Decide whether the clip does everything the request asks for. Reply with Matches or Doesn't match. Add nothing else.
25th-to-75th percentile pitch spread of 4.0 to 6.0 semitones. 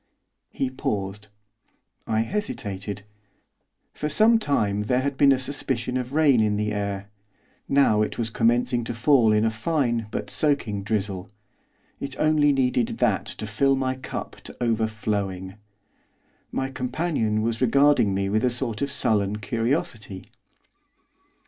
Matches